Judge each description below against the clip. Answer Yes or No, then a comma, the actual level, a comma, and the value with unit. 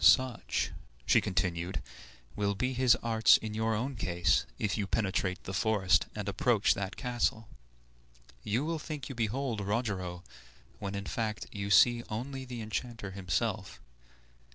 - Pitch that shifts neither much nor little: Yes, average, 3.9 semitones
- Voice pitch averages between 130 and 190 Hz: No, low, 105 Hz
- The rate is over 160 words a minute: No, average, 145 wpm